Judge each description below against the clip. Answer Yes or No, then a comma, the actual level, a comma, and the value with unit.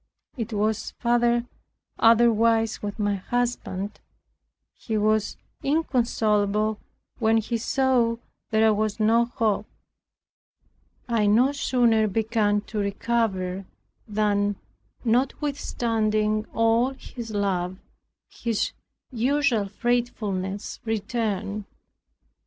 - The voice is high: Yes, high, 220 Hz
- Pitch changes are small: Yes, narrow, 2.3 semitones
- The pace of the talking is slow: Yes, slow, 85 wpm